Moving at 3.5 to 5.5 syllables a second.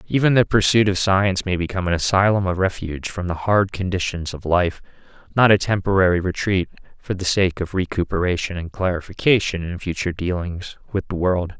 No: 5.7 syllables/s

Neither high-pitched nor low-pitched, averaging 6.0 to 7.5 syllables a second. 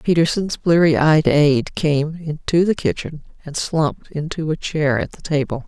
No: medium, 155 Hz; 4.5 syllables/s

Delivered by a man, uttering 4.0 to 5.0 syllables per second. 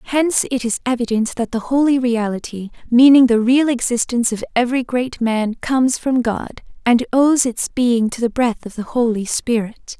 No: female; 4.9 syllables/s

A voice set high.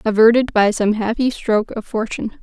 Yes: high, 220 Hz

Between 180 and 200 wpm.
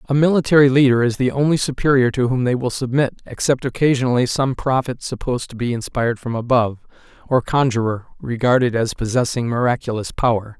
No: average, 165 wpm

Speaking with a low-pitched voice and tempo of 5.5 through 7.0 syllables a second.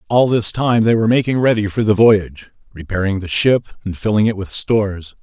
Yes: low, 105 Hz; 5.7 syllables/s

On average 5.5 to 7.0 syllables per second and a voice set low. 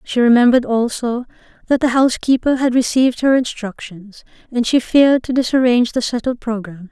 No: 5.9 syllables/s; high, 245 Hz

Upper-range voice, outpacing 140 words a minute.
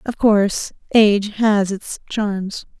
No: high, 205 Hz; slow, 130 wpm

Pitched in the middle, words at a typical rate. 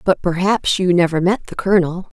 Yes: medium, 180 Hz; average, 190 wpm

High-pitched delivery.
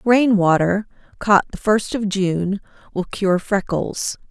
Yes: high, 200 Hz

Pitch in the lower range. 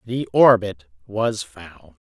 Yes: low, 105 Hz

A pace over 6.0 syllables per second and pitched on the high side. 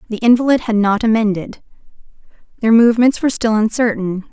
Yes: 6.2 syllables/s; high, 225 Hz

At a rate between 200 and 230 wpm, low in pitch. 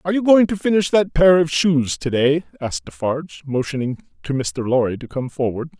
No: fast, 205 wpm; medium, 150 Hz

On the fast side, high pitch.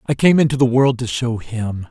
No: fast, 250 wpm; low, 125 Hz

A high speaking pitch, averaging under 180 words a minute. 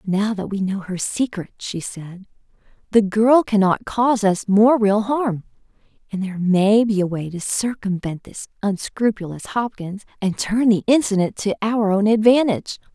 Yes: high, 205 Hz; average, 160 wpm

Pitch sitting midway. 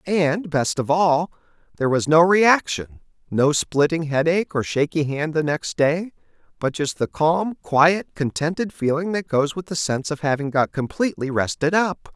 Yes: medium, 160 Hz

